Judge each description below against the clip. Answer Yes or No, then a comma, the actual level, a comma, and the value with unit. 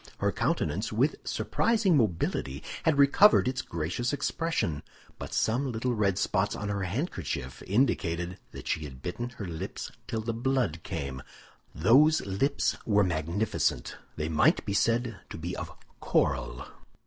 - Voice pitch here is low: Yes, low, 105 Hz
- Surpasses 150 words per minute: No, average, 145 wpm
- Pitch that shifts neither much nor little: No, wide, 7.5 semitones